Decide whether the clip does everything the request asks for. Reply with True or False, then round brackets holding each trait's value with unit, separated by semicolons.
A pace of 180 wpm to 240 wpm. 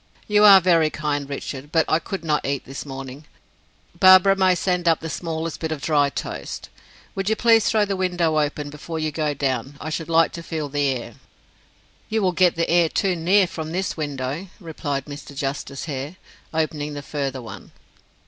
True (195 wpm)